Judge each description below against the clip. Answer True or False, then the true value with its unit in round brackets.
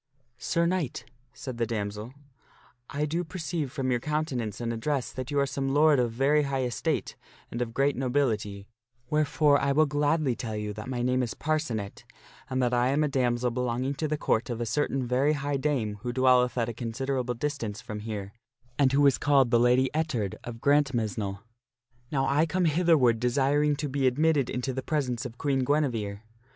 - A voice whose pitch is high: False (130 Hz)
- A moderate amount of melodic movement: True (3.5 semitones)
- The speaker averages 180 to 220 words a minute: True (195 wpm)